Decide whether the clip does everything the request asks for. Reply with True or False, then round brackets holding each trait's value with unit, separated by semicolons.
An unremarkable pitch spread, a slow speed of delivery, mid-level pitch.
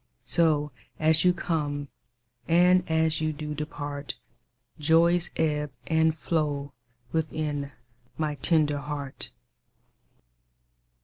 False (1.6 semitones; 90 wpm; 155 Hz)